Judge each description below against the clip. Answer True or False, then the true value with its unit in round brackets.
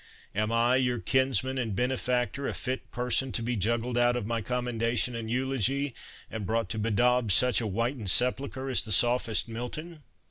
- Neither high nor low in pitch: False (120 Hz)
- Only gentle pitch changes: True (2.0 semitones)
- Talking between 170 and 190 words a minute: True (175 wpm)